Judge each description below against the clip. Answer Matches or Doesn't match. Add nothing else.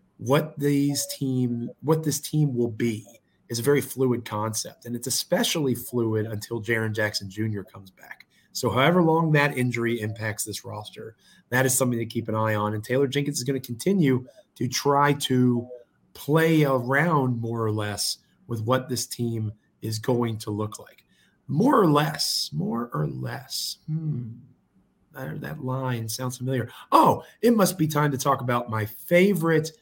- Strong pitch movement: Doesn't match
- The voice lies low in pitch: Matches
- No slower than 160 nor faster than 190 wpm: Matches